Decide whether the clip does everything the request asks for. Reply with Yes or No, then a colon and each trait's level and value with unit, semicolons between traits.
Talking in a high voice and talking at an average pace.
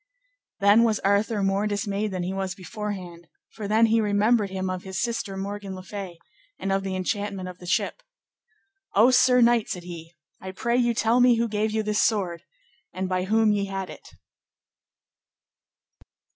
Yes: high, 200 Hz; average, 175 wpm